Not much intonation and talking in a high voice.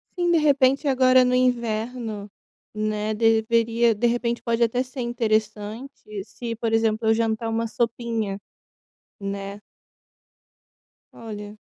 Yes: narrow, 2.2 semitones; high, 230 Hz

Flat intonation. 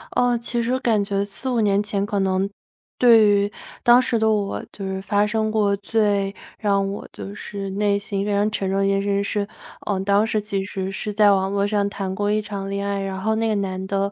Yes: narrow, 1.4 semitones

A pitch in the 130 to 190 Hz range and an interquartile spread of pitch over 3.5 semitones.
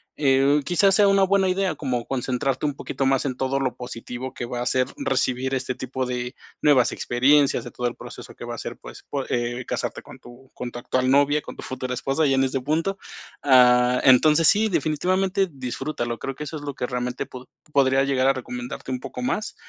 No: low, 135 Hz; average, 3.0 semitones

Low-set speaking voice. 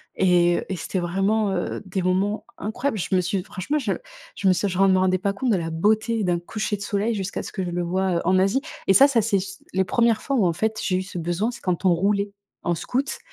No: high, 195 Hz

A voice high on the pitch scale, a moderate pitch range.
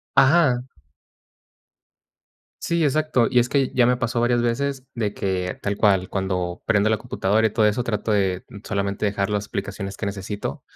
No: low, 110 Hz; average, 3.7 semitones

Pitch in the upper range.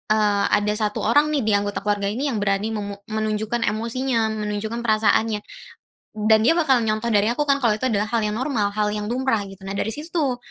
Yes: high, 215 Hz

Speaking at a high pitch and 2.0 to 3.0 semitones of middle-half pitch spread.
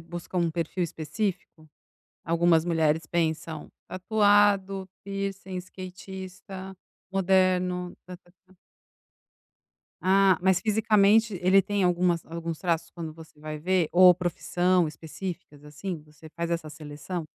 No: medium, 180 Hz; narrow, 2.6 semitones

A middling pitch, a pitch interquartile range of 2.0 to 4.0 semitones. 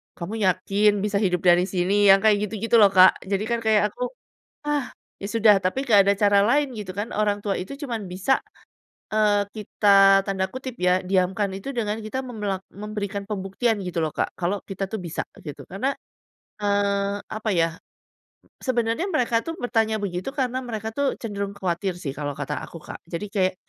No: high, 205 Hz; average, 2.8 semitones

